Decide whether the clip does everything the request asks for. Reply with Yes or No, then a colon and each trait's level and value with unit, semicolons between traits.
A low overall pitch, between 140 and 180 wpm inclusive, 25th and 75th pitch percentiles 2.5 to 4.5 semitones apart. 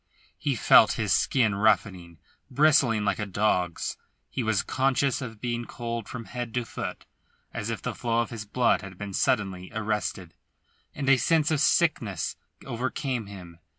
Yes: low, 115 Hz; average, 160 wpm; average, 3.8 semitones